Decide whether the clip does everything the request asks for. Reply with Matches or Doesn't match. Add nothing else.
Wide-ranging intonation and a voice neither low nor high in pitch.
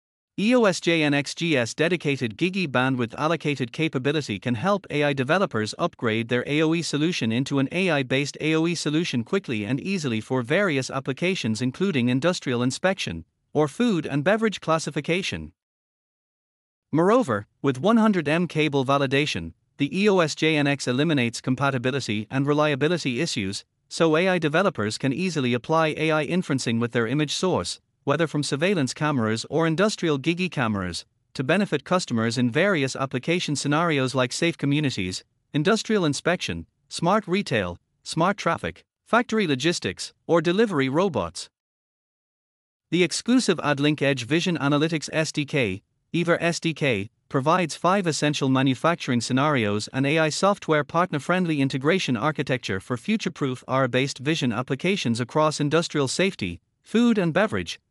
Doesn't match